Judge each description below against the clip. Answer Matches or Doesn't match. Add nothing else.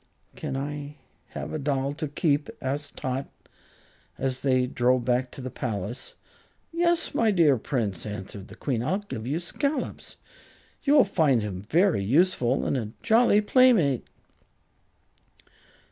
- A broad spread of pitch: Matches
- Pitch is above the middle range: Doesn't match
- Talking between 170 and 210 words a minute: Doesn't match